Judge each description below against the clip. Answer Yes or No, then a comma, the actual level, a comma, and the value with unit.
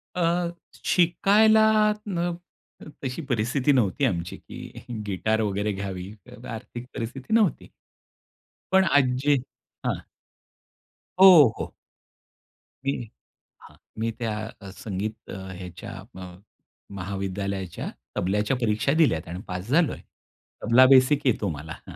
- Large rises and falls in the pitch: Yes, wide, 6.9 semitones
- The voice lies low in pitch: Yes, low, 115 Hz